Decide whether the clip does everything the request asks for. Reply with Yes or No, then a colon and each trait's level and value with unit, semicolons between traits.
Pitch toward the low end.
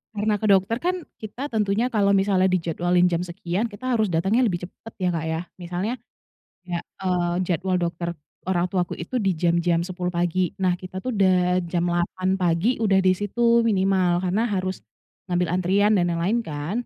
No: medium, 185 Hz